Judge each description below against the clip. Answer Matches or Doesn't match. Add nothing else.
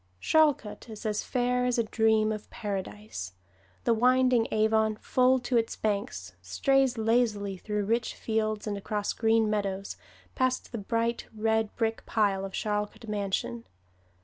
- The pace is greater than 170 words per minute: Doesn't match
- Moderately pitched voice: Doesn't match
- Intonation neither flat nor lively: Doesn't match